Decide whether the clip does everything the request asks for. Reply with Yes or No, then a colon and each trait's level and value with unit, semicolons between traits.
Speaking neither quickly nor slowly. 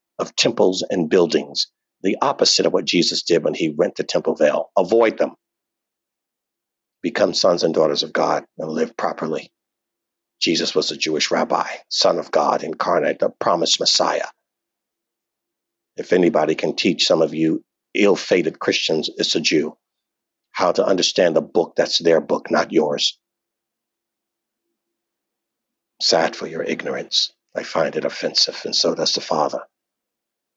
Yes: average, 150 wpm